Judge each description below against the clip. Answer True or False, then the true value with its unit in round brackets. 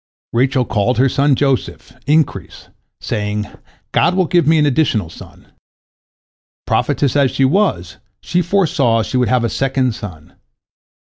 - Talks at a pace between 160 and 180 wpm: False (145 wpm)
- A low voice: True (130 Hz)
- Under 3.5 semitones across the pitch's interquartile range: False (4.8 semitones)